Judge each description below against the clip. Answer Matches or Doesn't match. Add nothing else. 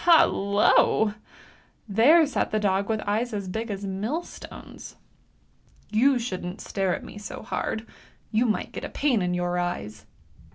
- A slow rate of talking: Doesn't match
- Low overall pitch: Doesn't match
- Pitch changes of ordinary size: Matches